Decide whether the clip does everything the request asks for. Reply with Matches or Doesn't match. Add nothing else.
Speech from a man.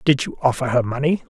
Matches